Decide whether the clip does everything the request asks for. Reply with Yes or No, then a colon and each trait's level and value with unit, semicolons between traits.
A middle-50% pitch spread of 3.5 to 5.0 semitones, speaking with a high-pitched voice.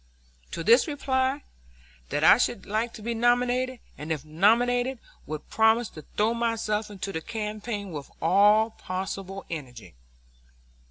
Yes: average, 4.4 semitones; high, 215 Hz